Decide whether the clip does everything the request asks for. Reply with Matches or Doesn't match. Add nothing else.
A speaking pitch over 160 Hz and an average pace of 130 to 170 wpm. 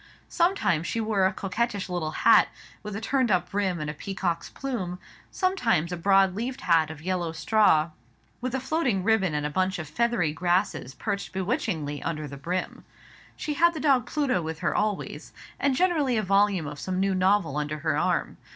Doesn't match